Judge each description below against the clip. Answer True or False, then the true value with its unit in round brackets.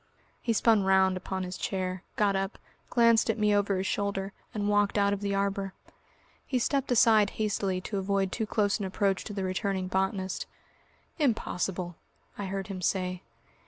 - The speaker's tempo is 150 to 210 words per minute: True (170 wpm)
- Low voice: False (195 Hz)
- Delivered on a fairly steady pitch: True (1.6 semitones)